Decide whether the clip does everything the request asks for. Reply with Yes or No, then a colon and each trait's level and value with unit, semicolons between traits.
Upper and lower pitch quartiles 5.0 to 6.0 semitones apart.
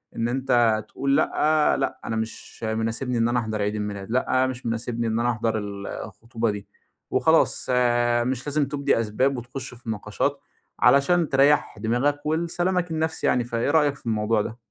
No: average, 3.7 semitones